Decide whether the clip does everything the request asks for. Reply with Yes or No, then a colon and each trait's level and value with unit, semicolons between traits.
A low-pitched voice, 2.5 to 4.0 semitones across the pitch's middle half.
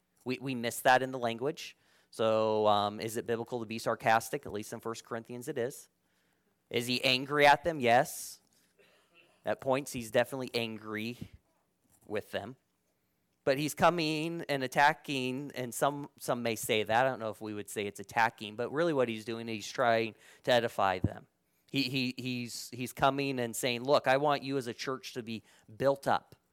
Yes: low, 120 Hz; average, 3.5 semitones